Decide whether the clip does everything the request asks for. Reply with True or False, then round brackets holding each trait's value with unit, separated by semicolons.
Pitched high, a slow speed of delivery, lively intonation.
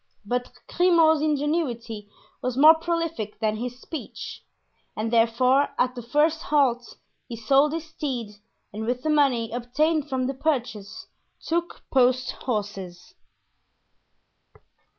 False (255 Hz; 120 wpm; 4.8 semitones)